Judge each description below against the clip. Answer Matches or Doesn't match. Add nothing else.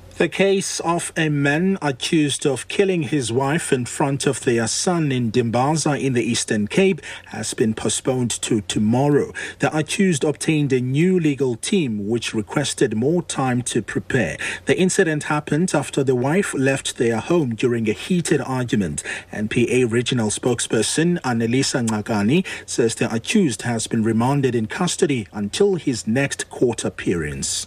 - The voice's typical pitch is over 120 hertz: Matches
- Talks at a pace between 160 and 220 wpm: Doesn't match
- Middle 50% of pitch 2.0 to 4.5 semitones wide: Doesn't match